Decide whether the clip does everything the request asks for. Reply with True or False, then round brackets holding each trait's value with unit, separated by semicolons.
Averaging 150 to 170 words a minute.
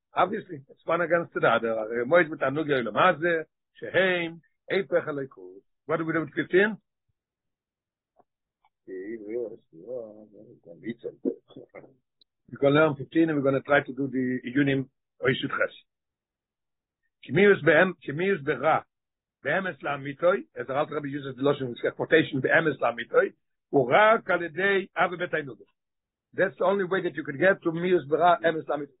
True (155 wpm)